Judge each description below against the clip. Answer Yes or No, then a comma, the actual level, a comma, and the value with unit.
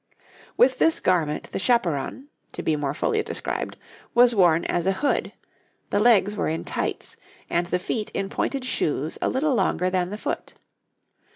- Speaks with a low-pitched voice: No, high, 190 Hz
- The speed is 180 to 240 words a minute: No, average, 170 wpm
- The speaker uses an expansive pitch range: Yes, wide, 6.0 semitones